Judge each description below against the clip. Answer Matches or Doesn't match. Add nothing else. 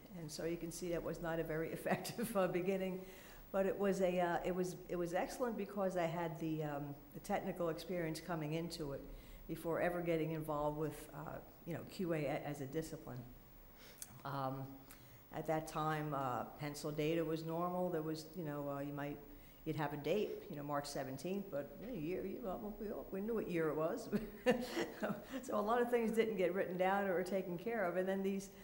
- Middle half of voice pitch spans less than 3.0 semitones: Doesn't match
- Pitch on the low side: Doesn't match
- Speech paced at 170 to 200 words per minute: Matches